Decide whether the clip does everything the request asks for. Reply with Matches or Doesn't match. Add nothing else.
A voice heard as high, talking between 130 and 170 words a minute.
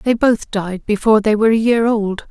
Doesn't match